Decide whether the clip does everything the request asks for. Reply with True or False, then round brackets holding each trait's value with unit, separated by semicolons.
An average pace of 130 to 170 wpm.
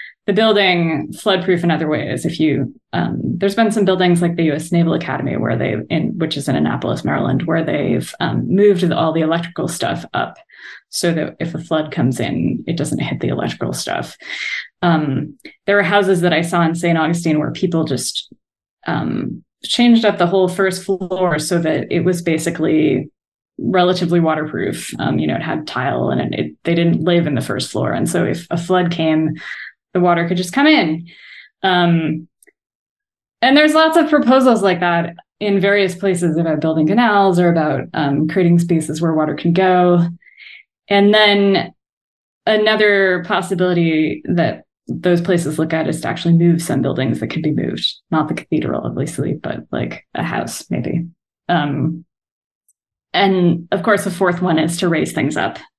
False (180 wpm)